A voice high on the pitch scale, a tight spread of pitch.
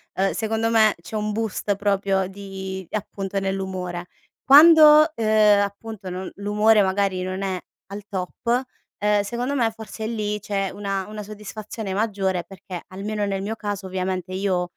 Yes: high, 200 Hz; narrow, 2.1 semitones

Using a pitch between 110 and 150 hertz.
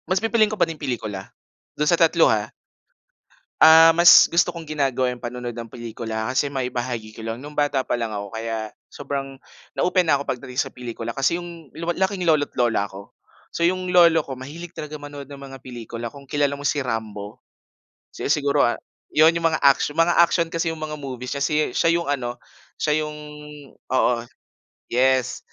Yes: medium, 140 Hz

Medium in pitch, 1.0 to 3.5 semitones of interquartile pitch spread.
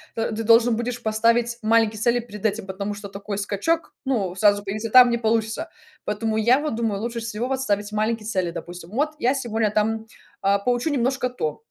No: high, 225 Hz; narrow, 2.5 semitones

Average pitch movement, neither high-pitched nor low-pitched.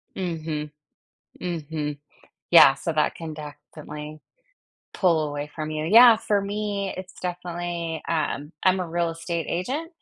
Yes: average, 3.0 semitones; medium, 165 Hz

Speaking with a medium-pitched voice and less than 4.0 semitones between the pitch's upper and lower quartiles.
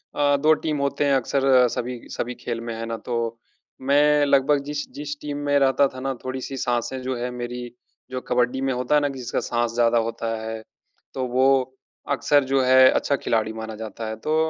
No: low, 130 Hz; average, 2.9 semitones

